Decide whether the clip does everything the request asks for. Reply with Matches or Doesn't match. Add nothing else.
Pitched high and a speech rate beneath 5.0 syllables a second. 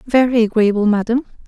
Doesn't match